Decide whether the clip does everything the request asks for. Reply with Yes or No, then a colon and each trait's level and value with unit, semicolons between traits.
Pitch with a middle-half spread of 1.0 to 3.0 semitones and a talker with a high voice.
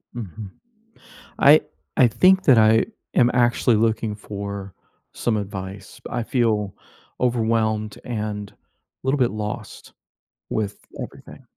No: narrow, 2.6 semitones; low, 110 Hz